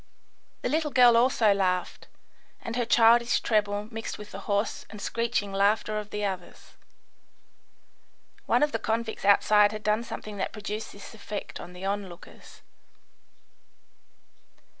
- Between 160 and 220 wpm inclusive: No, average, 140 wpm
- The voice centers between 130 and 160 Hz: No, high, 210 Hz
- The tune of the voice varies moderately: No, narrow, 2.3 semitones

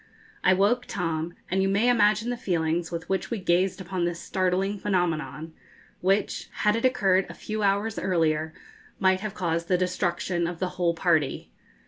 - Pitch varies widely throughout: No, average, 2.7 semitones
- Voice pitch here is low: No, medium, 185 Hz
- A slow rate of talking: No, average, 170 wpm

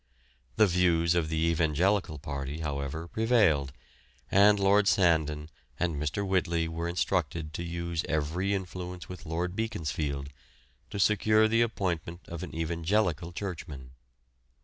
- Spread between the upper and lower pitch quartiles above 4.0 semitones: No, average, 3.5 semitones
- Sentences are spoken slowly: Yes, slow, 125 wpm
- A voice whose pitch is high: No, very low, 85 Hz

